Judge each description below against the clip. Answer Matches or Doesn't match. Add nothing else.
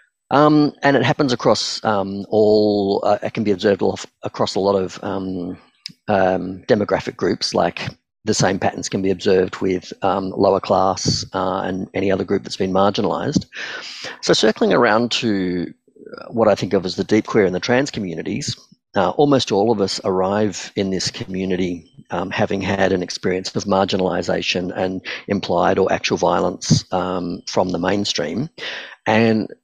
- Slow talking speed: Doesn't match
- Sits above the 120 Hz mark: Doesn't match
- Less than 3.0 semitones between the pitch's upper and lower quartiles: Matches